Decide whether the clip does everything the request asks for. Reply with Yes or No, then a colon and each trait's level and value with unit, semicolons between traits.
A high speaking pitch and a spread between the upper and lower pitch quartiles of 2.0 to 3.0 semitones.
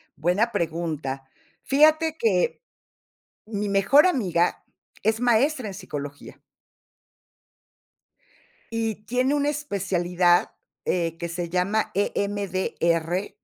No: high, 200 Hz; average, 5.2 semitones